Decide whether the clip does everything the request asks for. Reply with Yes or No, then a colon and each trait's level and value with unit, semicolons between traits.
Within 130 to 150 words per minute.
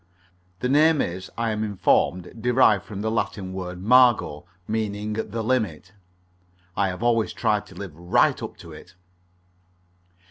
Yes: average, 145 wpm